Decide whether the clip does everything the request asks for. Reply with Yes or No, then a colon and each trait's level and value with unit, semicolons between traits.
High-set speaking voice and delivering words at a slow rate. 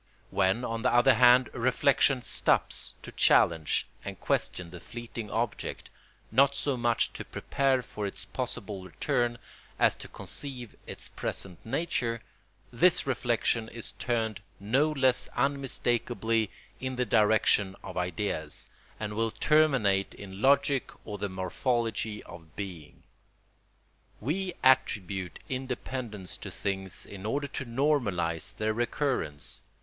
No: low, 115 Hz; slow, 125 wpm